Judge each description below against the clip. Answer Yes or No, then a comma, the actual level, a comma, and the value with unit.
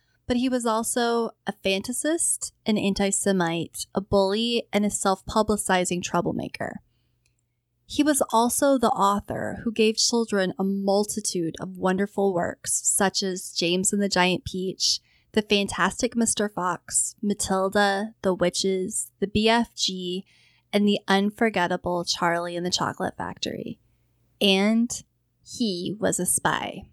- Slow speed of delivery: Yes, slow, 130 wpm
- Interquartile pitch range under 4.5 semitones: Yes, average, 3.4 semitones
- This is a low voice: No, high, 195 Hz